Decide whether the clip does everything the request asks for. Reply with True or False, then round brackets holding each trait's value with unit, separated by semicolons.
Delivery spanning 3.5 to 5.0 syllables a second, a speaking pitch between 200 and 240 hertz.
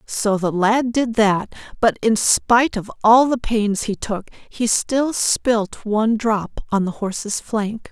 True (3.6 syllables/s; 220 Hz)